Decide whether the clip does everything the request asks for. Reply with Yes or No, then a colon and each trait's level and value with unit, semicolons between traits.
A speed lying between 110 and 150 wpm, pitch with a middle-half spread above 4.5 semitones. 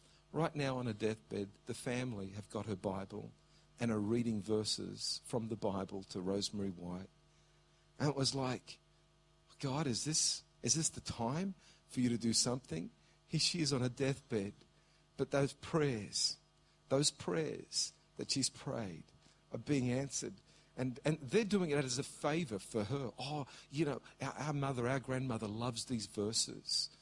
No: average, 165 wpm; average, 5.1 semitones